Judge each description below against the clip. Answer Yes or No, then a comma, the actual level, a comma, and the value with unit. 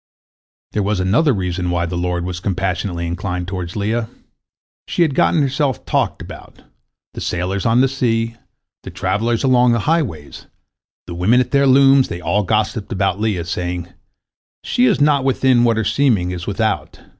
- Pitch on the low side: Yes, low, 105 Hz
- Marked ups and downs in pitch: Yes, wide, 6.0 semitones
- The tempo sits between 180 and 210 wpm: No, average, 165 wpm